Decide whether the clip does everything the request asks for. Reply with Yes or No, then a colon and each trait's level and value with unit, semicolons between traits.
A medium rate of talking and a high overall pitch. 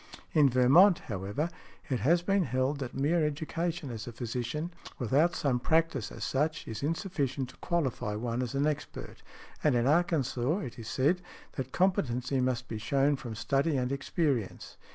No: average, 165 wpm; low, 135 Hz